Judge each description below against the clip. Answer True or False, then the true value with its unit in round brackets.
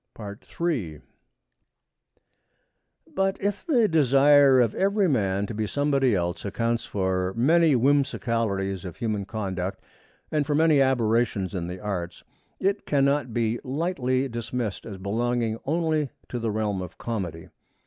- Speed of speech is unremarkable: False (130 wpm)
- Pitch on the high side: False (120 Hz)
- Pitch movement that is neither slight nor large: False (6.2 semitones)